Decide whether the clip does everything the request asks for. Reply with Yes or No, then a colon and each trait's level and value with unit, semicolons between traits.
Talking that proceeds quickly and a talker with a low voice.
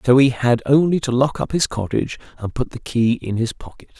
Yes: fast, 240 wpm; low, 125 Hz